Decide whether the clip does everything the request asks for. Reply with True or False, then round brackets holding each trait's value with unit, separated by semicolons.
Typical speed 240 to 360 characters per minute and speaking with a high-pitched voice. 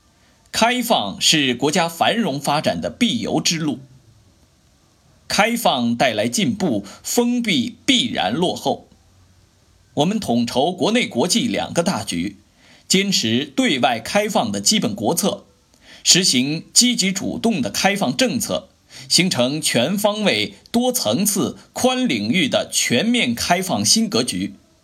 False (190 characters per minute; 205 Hz)